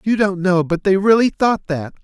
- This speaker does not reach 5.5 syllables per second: Yes, 4.8 syllables/s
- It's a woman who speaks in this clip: No, male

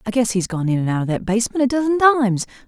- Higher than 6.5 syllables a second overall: Yes, 7.1 syllables/s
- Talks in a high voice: Yes, high, 225 Hz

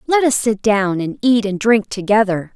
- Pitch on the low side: No, high, 215 Hz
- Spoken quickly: Yes, fast, 210 wpm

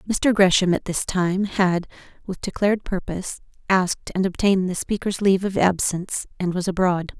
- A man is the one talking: No, female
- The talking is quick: No, average, 165 wpm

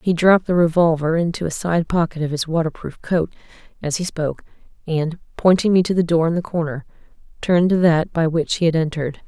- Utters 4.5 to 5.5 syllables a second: No, 6.0 syllables/s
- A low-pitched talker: No, medium, 165 Hz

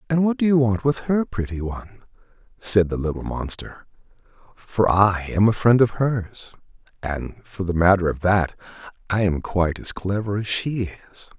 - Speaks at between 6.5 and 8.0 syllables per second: No, 5.0 syllables/s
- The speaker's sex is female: No, male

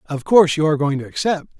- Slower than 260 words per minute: No, fast, 265 wpm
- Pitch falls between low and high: Yes, medium, 155 Hz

